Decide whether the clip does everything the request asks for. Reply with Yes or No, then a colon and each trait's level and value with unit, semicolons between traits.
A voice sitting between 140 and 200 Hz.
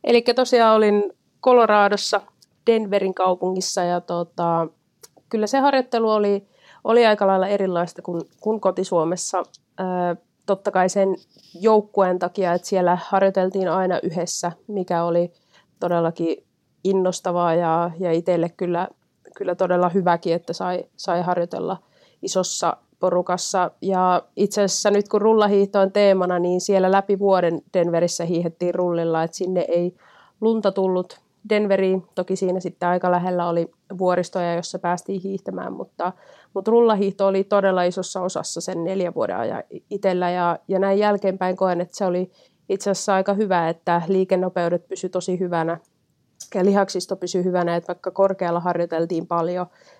Yes: medium, 185 Hz